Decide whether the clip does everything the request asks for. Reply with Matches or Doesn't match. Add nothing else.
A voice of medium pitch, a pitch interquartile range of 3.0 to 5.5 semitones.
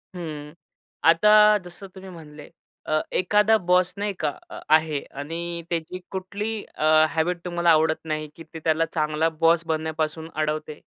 Doesn't match